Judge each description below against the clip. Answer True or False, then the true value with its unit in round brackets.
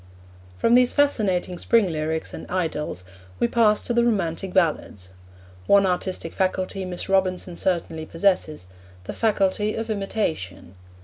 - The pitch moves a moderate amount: True (4.2 semitones)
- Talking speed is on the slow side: True (130 wpm)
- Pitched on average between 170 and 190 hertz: True (185 Hz)